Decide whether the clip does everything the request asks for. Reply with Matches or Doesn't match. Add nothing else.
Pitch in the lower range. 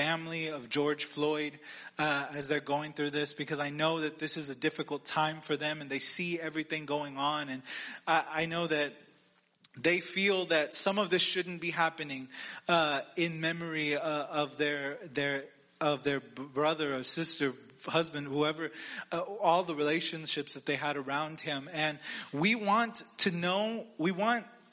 Doesn't match